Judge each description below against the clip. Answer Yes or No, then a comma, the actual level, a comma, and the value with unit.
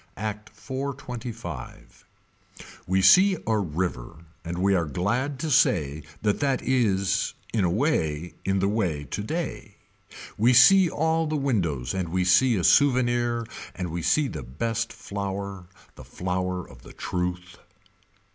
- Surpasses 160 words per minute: No, average, 140 wpm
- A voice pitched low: Yes, low, 100 Hz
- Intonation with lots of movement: Yes, wide, 6.0 semitones